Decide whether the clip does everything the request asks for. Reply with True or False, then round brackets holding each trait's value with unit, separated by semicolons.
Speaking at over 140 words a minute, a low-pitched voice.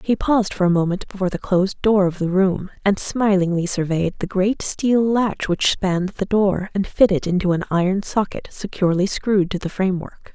False (195 wpm; 190 Hz)